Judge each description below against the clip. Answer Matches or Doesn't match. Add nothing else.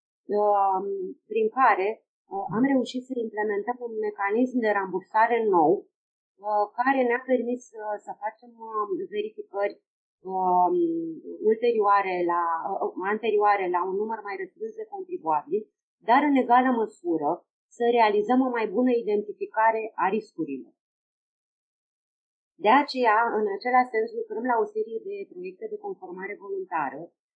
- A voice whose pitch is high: Matches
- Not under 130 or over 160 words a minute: Doesn't match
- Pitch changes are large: Matches